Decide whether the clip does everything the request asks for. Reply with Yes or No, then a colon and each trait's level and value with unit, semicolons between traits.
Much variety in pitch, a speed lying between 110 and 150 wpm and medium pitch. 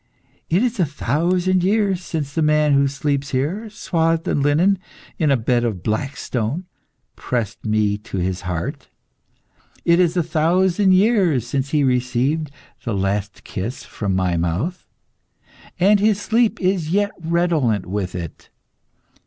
Yes: wide, 7.8 semitones; average, 145 wpm; medium, 150 Hz